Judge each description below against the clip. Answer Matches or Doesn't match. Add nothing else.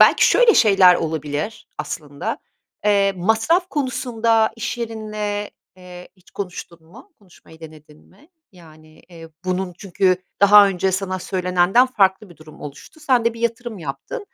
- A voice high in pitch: Matches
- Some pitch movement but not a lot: Matches